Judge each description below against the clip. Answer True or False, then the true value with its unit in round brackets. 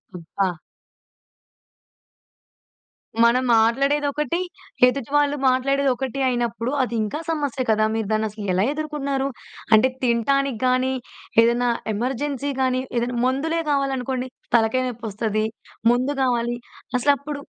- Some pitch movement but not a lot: True (3.0 semitones)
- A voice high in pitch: True (255 Hz)